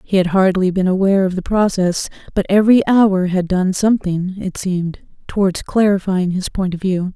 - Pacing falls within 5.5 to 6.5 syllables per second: No, 5.3 syllables/s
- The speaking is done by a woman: Yes, female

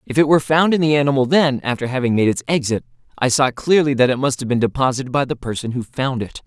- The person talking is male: Yes, male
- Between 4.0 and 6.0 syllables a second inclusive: No, 6.6 syllables/s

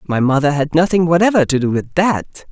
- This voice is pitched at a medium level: Yes, medium, 155 Hz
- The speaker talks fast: Yes, fast, 215 wpm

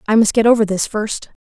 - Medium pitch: No, high, 215 Hz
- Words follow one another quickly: Yes, fast, 250 wpm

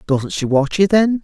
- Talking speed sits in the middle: No, fast, 245 wpm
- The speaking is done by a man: Yes, male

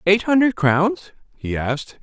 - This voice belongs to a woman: No, male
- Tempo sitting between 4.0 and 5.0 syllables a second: Yes, 4.1 syllables/s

